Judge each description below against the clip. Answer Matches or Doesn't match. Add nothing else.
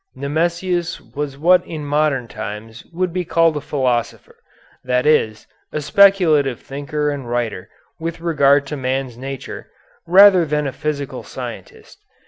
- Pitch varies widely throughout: Doesn't match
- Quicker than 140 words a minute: Doesn't match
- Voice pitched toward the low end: Doesn't match